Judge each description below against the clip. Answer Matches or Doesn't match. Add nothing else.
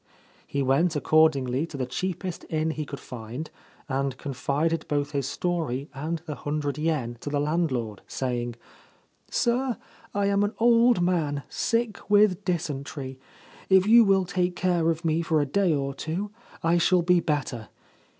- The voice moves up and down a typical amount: Matches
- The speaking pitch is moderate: Matches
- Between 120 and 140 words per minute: Doesn't match